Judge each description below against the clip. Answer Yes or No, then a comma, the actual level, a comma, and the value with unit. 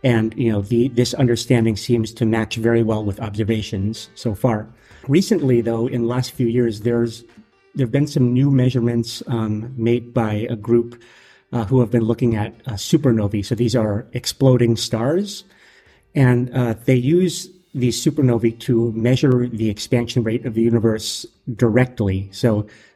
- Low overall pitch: Yes, low, 120 Hz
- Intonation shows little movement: Yes, narrow, 1.9 semitones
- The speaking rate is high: No, average, 165 wpm